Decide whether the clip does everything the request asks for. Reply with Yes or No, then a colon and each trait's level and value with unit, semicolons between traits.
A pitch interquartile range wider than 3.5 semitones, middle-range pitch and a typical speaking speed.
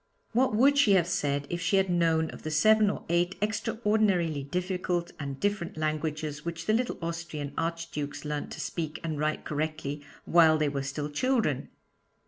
Yes: average, 4.1 semitones; medium, 165 Hz; average, 170 wpm